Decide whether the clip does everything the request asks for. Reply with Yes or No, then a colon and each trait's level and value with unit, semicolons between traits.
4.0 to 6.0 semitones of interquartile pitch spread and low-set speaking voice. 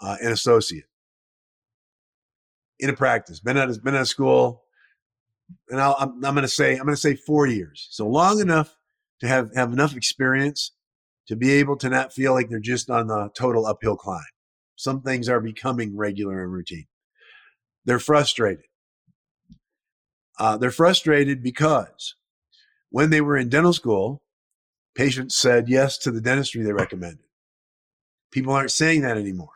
Yes: average, 4.3 semitones; low, 130 Hz